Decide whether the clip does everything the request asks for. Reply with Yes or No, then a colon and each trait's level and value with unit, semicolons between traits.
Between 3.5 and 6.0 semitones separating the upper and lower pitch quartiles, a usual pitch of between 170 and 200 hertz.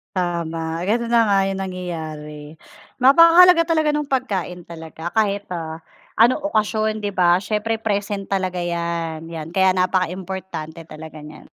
Yes: average, 4.6 semitones; medium, 185 Hz